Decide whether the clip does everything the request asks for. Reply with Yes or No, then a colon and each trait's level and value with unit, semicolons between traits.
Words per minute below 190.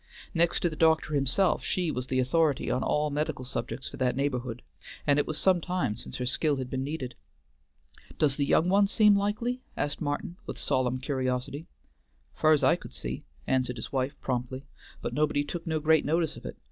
No: average, 195 wpm